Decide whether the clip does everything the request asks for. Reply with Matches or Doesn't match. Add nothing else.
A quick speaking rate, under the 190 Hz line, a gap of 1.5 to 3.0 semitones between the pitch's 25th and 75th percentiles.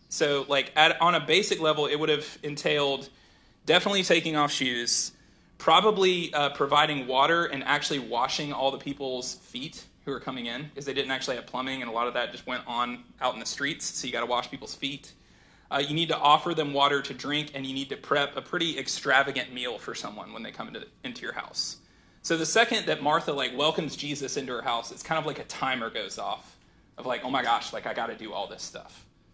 Matches